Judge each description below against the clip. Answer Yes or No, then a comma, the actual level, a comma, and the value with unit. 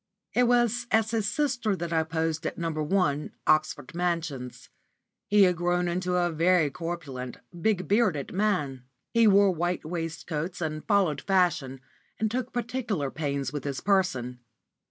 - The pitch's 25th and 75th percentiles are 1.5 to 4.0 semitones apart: No, average, 4.9 semitones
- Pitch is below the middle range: No, medium, 175 Hz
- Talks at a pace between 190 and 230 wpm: No, average, 150 wpm